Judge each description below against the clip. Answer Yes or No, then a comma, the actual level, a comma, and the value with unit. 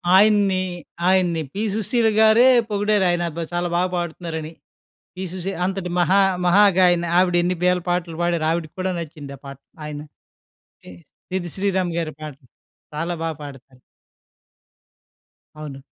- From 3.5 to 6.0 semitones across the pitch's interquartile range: No, average, 2.8 semitones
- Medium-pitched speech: Yes, medium, 175 Hz